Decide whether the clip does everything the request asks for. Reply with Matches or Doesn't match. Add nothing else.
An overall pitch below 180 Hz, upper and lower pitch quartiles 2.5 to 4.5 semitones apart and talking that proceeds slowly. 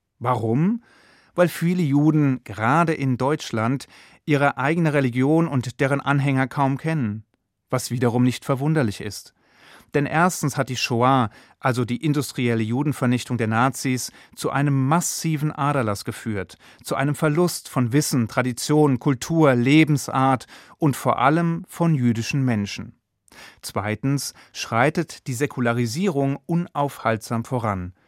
Matches